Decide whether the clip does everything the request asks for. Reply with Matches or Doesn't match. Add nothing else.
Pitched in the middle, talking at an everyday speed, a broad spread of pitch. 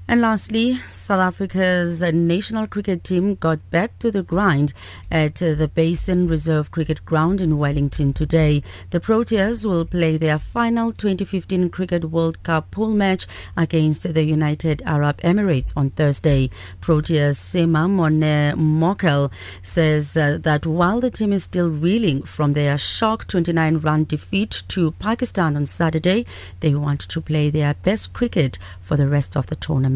Doesn't match